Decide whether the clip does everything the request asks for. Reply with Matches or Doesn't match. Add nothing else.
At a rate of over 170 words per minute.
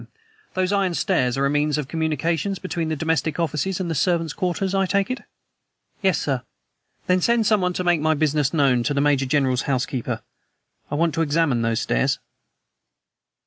Matches